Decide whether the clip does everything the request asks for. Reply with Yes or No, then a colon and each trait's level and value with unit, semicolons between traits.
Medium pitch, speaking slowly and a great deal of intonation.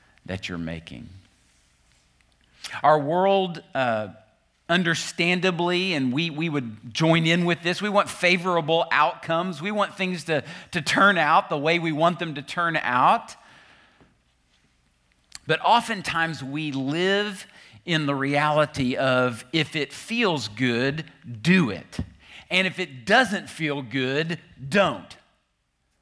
Yes: medium, 150 Hz; slow, 125 wpm; wide, 6.7 semitones